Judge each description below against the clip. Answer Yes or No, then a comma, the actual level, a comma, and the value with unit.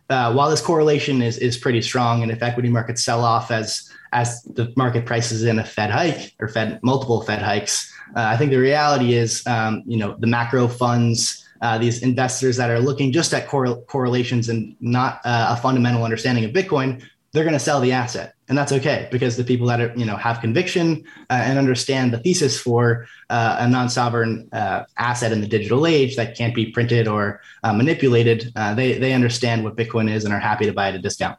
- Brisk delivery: Yes, fast, 215 wpm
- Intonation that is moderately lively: No, narrow, 2.1 semitones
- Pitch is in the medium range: No, low, 120 Hz